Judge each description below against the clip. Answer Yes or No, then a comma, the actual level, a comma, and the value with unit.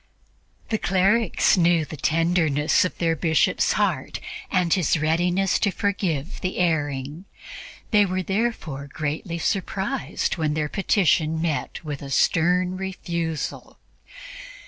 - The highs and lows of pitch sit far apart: No, average, 3.4 semitones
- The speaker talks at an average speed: No, slow, 120 wpm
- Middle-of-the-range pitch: Yes, medium, 170 Hz